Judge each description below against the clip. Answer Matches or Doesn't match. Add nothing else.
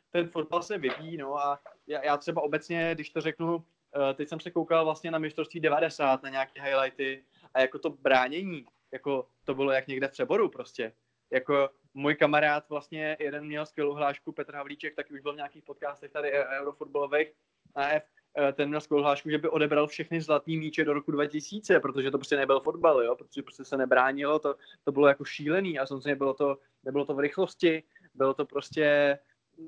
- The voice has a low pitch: Doesn't match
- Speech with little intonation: Matches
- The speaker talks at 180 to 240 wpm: Matches